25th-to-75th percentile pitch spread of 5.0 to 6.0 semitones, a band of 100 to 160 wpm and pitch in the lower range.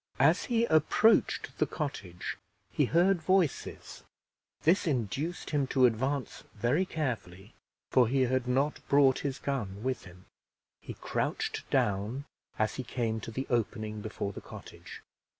Yes: average, 5.3 semitones; average, 140 wpm; low, 130 Hz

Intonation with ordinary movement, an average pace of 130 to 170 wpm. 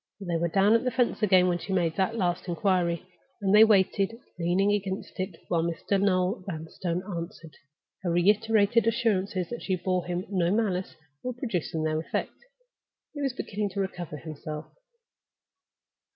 Yes: average, 3.1 semitones; average, 155 wpm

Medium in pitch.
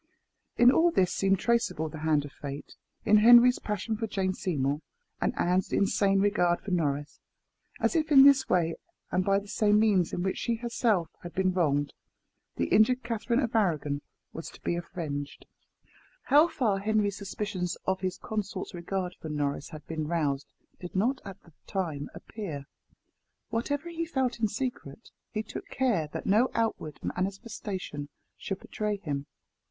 No: high, 195 Hz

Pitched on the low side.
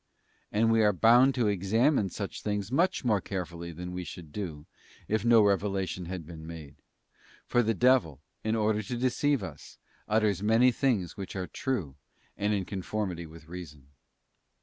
Yes: low, 100 Hz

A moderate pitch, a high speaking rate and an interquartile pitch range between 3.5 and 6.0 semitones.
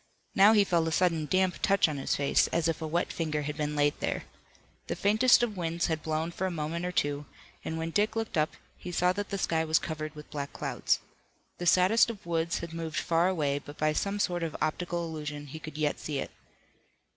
No: medium, 165 Hz; fast, 225 wpm; average, 2.8 semitones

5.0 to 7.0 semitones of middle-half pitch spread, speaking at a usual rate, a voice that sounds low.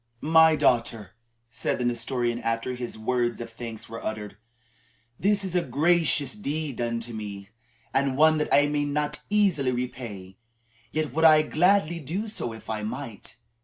Yes: average, 5.3 semitones; average, 165 wpm; low, 125 Hz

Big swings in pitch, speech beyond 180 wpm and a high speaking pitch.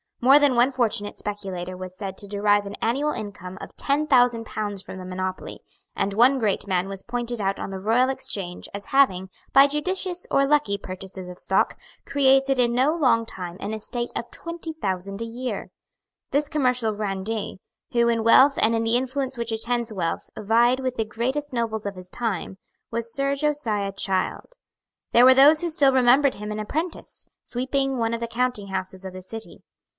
No: average, 4.9 semitones; average, 190 wpm; high, 230 Hz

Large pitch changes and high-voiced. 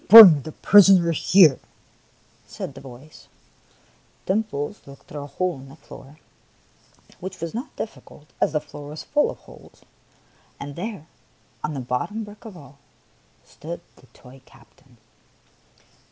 No: wide, 5.7 semitones; medium, 155 Hz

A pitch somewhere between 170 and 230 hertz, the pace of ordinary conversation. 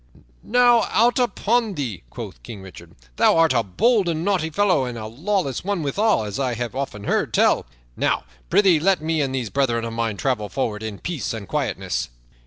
No: medium, 140 Hz; average, 195 wpm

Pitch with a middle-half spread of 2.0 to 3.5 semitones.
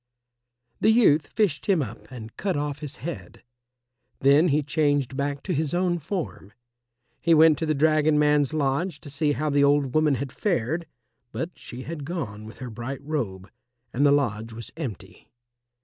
Yes: average, 2.9 semitones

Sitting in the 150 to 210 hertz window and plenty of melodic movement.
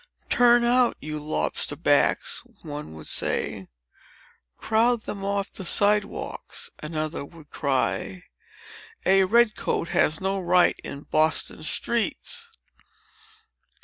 Yes: high, 190 Hz; wide, 6.3 semitones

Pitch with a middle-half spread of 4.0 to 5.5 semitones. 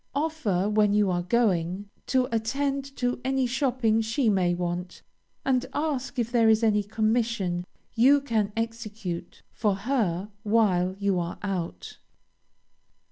Yes: average, 4.5 semitones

